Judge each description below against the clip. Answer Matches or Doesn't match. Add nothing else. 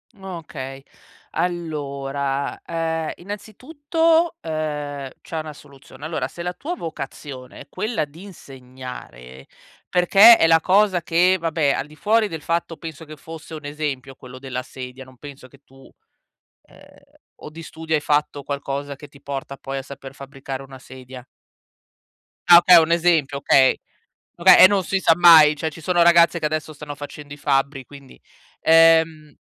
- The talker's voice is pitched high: Doesn't match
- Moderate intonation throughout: Matches